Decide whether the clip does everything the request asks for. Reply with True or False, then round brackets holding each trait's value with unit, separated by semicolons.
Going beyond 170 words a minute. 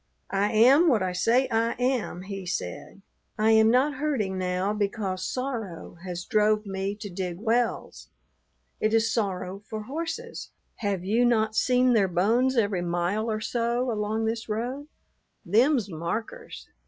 False (150 wpm)